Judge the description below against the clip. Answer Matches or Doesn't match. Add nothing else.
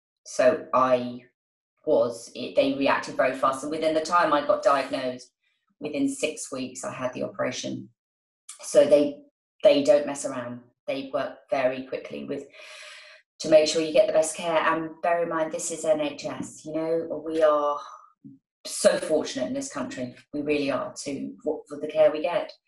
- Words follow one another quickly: Doesn't match